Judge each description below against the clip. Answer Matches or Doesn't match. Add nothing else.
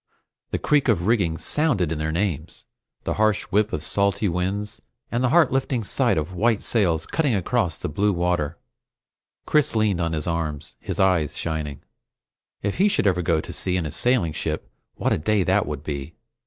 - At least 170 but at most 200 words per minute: Matches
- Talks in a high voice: Doesn't match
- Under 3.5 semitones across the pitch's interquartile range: Doesn't match